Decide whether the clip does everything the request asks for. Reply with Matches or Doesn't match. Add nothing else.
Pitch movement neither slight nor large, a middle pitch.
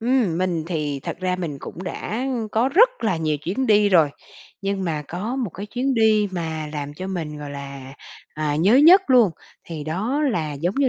Doesn't match